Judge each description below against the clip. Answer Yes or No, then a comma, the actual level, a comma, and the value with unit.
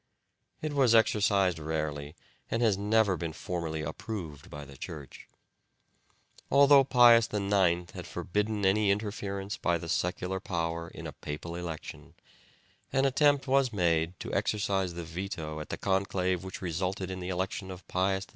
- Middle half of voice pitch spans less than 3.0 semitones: No, average, 3.8 semitones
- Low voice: Yes, very low, 95 Hz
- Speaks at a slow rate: No, average, 155 wpm